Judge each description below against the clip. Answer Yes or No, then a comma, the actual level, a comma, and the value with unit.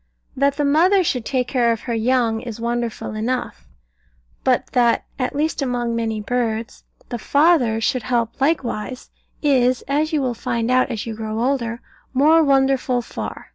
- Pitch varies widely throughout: No, average, 3.0 semitones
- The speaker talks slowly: No, average, 165 wpm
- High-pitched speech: Yes, very high, 250 Hz